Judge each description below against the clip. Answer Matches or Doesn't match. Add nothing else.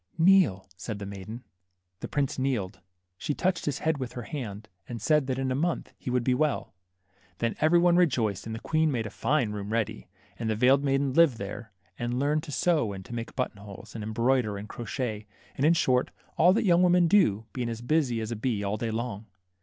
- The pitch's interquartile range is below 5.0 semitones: Doesn't match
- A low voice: Matches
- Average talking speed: Doesn't match